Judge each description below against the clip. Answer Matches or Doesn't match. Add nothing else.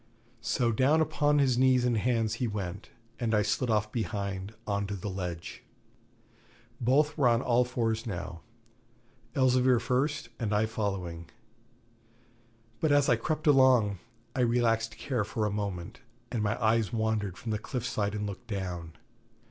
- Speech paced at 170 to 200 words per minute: Doesn't match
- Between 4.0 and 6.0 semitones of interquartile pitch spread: Doesn't match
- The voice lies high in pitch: Doesn't match